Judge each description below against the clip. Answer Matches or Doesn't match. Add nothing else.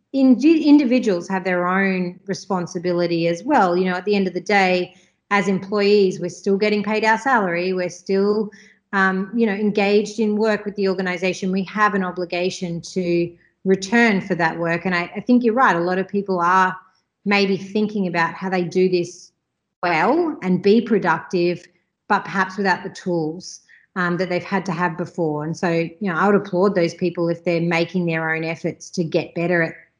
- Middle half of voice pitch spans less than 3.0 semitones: Matches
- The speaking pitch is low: Doesn't match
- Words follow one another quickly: Doesn't match